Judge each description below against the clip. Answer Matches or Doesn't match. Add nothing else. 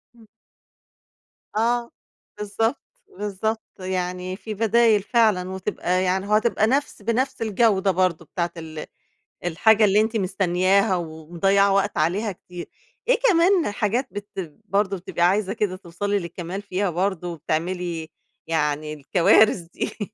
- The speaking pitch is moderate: Doesn't match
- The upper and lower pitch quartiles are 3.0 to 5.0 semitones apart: Matches